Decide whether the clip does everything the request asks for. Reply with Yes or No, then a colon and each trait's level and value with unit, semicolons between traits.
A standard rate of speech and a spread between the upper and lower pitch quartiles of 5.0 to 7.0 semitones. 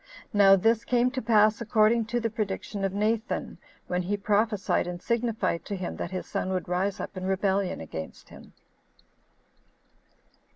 No: average, 160 wpm; average, 3.0 semitones